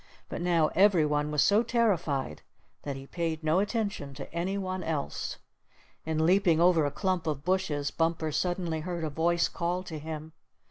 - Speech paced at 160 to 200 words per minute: Yes, average, 175 wpm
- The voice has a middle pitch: Yes, medium, 165 Hz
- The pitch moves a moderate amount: Yes, average, 3.1 semitones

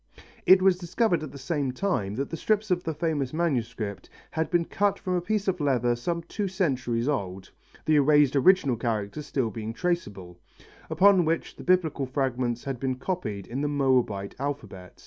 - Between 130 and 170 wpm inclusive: No, average, 180 wpm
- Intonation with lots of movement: Yes, wide, 6.6 semitones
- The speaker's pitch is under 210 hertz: Yes, medium, 140 Hz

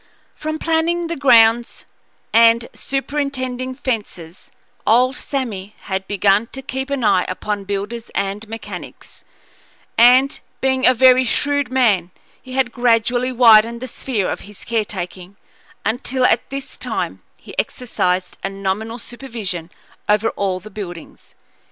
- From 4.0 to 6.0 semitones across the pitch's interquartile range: Yes, average, 4.3 semitones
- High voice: Yes, high, 235 Hz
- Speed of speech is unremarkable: No, slow, 130 wpm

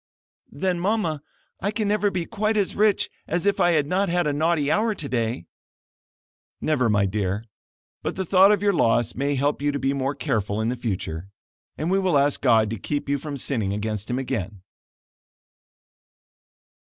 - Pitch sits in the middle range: Yes, medium, 145 Hz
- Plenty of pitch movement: Yes, wide, 8.4 semitones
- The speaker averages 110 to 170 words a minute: No, average, 180 wpm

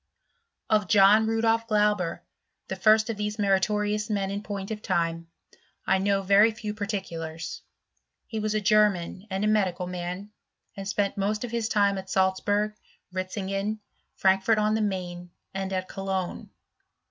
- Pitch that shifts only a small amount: Yes, narrow, 2.0 semitones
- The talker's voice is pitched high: Yes, high, 200 Hz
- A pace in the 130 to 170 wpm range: Yes, average, 160 wpm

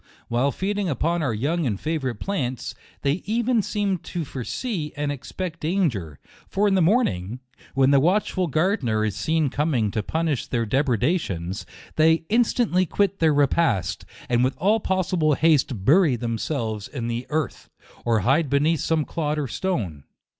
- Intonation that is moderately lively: No, wide, 6.8 semitones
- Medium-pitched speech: Yes, medium, 150 Hz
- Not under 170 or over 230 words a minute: No, average, 160 wpm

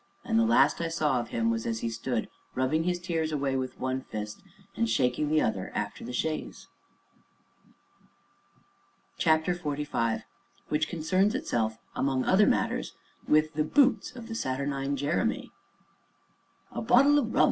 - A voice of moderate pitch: Yes, medium, 150 Hz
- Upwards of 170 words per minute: No, average, 150 wpm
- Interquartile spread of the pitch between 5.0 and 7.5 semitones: Yes, wide, 5.6 semitones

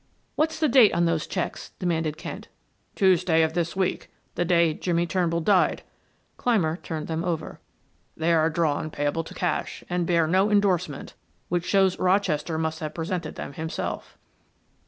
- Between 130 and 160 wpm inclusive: Yes, average, 155 wpm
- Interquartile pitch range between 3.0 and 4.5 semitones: No, narrow, 2.4 semitones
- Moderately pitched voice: Yes, medium, 170 Hz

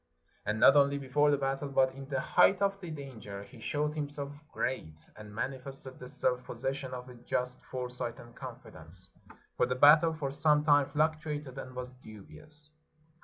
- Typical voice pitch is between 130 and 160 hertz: Yes, low, 135 Hz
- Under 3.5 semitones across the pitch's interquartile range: Yes, average, 2.9 semitones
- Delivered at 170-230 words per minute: Yes, average, 175 wpm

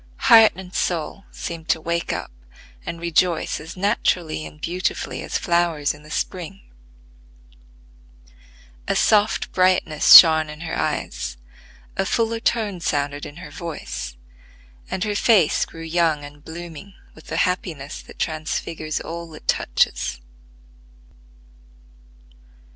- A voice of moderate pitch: Yes, medium, 170 Hz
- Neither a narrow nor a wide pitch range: Yes, average, 3.0 semitones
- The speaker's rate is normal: No, slow, 125 wpm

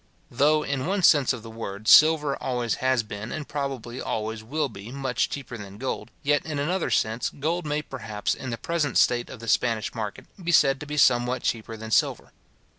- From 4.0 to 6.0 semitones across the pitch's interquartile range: Yes, average, 4.6 semitones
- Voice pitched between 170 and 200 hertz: No, low, 130 Hz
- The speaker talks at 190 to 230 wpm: Yes, average, 200 wpm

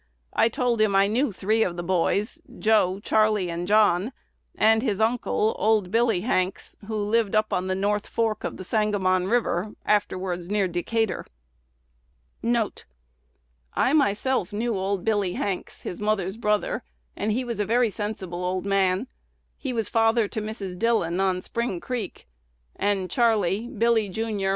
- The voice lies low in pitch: No, high, 210 Hz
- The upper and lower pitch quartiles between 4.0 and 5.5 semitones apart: No, average, 3.3 semitones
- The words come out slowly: No, average, 155 wpm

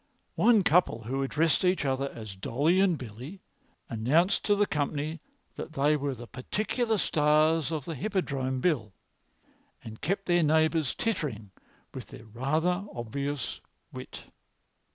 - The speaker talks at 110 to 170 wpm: Yes, slow, 135 wpm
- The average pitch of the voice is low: No, medium, 150 Hz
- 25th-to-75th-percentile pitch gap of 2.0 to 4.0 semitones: No, average, 5.2 semitones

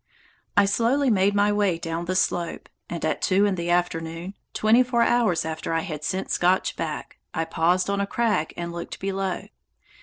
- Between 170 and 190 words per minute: Yes, average, 185 wpm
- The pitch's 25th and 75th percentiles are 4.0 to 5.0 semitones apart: No, average, 3.4 semitones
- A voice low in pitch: No, medium, 185 Hz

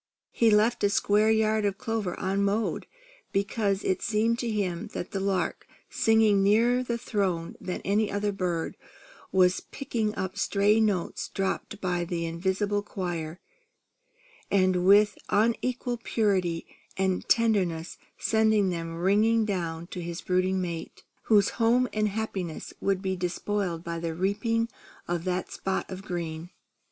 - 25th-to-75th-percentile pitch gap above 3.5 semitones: No, average, 3.2 semitones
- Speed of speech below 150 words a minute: Yes, average, 140 wpm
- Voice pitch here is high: Yes, high, 195 Hz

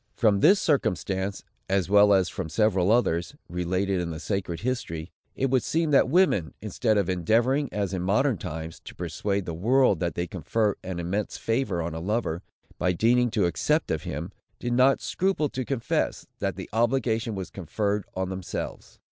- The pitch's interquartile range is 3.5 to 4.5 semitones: No, average, 5.1 semitones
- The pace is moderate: Yes, average, 180 wpm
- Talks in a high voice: No, low, 100 Hz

